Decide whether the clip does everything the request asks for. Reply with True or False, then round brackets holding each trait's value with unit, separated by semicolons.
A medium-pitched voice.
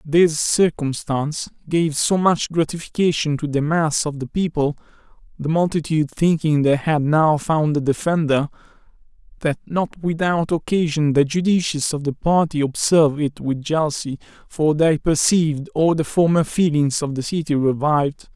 True (155 Hz)